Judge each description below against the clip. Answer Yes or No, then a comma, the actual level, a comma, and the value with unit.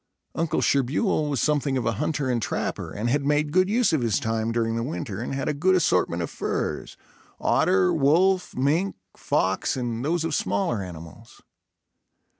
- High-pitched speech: No, low, 135 Hz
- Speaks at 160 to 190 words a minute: Yes, average, 175 wpm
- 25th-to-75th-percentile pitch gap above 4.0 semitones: Yes, wide, 5.5 semitones